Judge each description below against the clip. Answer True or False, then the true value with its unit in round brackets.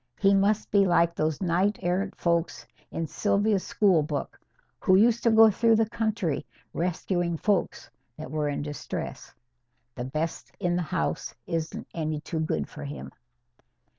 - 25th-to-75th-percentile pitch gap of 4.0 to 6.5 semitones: True (4.4 semitones)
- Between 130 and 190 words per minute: True (155 wpm)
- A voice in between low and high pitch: True (175 Hz)